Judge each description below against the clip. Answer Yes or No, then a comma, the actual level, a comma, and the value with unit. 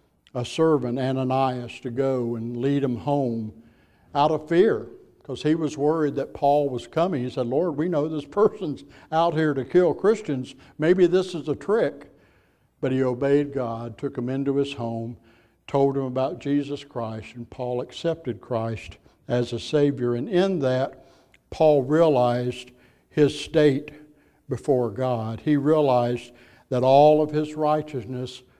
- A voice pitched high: No, low, 135 Hz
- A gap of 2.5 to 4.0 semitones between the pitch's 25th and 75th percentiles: Yes, average, 3.6 semitones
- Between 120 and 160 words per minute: Yes, average, 155 wpm